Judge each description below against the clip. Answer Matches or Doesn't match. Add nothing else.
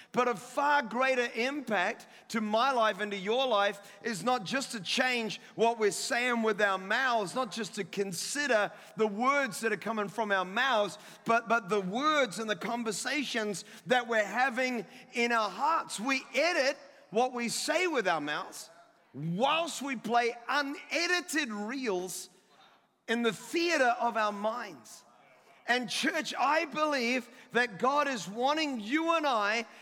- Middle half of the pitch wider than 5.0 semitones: Doesn't match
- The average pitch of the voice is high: Matches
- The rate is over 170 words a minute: Doesn't match